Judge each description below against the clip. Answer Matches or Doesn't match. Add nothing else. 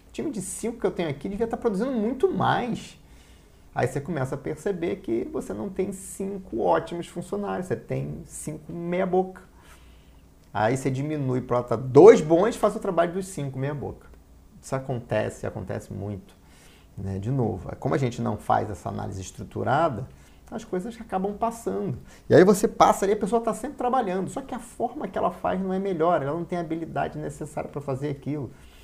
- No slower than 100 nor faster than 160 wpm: Doesn't match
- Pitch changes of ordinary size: Doesn't match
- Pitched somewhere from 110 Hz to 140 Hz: Doesn't match